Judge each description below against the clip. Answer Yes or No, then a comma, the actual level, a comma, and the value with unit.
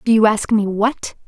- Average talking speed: No, fast, 235 wpm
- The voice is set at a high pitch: Yes, high, 215 Hz